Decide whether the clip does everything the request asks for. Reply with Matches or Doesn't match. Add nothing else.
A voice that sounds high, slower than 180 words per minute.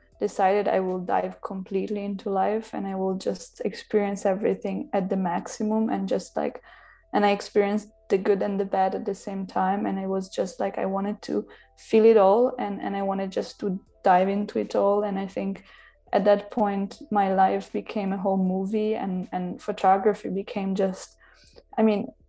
Doesn't match